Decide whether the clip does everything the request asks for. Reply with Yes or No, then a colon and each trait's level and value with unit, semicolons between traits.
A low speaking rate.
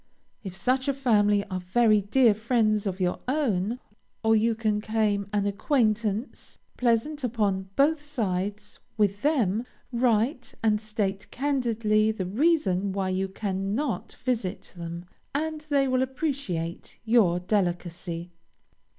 Yes: slow, 125 wpm